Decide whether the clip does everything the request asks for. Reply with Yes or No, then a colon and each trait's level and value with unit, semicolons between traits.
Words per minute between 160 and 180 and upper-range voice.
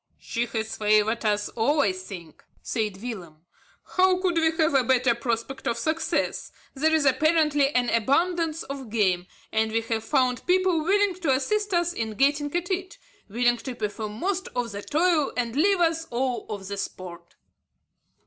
Yes: average, 170 wpm; very high, 255 Hz